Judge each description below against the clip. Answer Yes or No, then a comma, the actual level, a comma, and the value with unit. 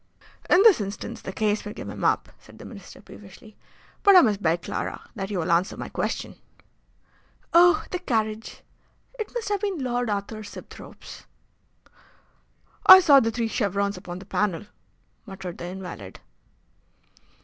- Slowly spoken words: No, average, 155 wpm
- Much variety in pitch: Yes, wide, 6.2 semitones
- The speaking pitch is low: No, high, 210 Hz